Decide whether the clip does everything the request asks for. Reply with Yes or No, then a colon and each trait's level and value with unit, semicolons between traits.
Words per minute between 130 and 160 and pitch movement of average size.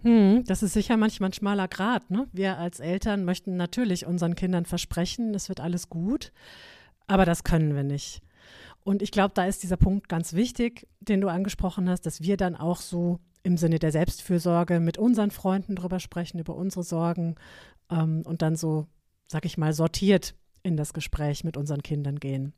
No: average, 185 wpm; average, 3.0 semitones